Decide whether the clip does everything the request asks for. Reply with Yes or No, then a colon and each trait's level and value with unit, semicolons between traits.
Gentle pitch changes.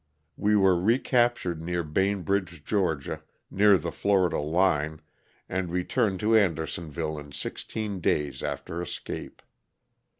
No: average, 4.0 semitones